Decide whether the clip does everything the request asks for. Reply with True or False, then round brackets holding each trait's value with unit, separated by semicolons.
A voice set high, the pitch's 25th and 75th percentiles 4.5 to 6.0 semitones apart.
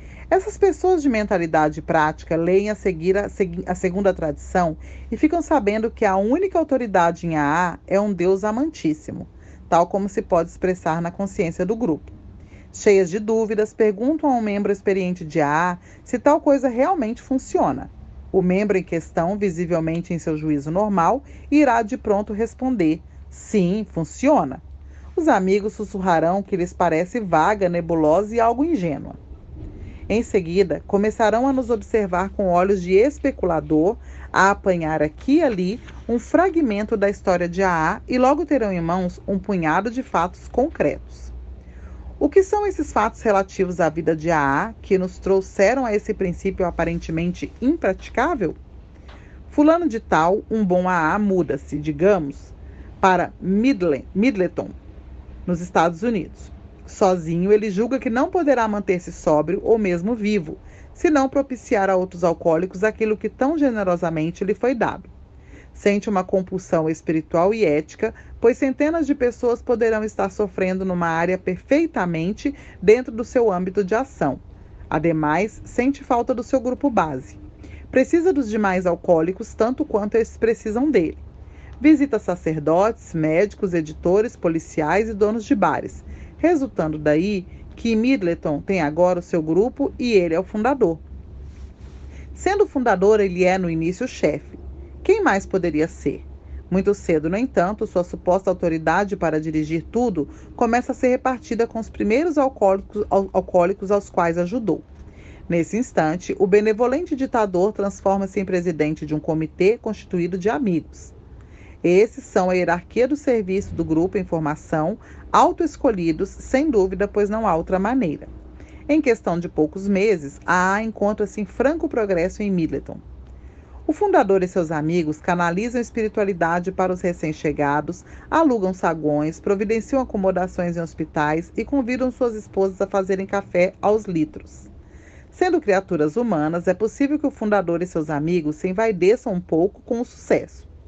True (195 Hz; 5.4 semitones)